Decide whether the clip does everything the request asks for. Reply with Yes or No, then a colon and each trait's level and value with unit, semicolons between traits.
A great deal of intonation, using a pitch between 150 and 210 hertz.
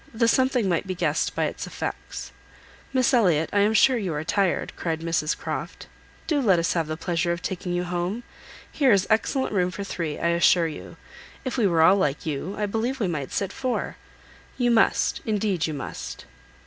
No: average, 4.9 semitones; medium, 185 Hz